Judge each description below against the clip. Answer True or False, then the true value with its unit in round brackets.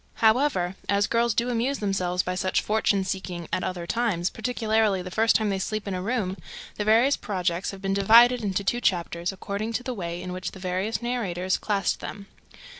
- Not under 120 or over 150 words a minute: False (195 wpm)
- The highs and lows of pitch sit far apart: False (3.6 semitones)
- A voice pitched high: True (200 Hz)